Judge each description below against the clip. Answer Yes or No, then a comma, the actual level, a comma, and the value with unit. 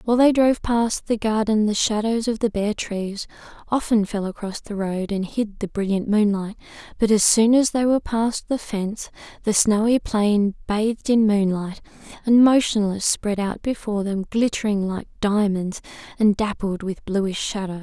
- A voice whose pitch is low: No, high, 210 Hz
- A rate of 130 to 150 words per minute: No, average, 170 wpm